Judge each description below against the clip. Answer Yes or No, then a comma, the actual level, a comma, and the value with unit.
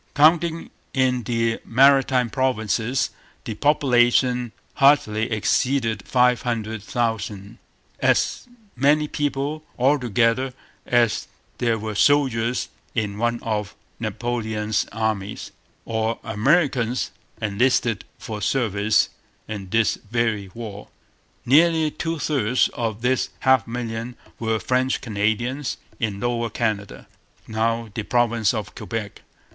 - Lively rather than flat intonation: No, average, 2.9 semitones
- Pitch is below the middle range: Yes, low, 115 Hz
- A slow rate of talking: Yes, slow, 105 wpm